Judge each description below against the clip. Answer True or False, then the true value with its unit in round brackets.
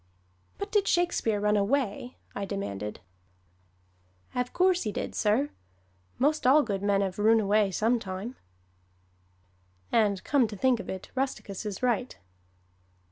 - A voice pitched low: False (220 Hz)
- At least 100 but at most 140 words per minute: True (135 wpm)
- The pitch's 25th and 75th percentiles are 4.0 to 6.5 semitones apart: True (4.5 semitones)